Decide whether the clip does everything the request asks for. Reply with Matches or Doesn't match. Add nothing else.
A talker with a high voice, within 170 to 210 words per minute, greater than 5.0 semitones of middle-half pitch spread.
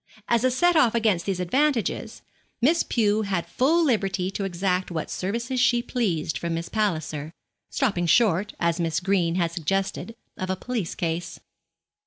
Doesn't match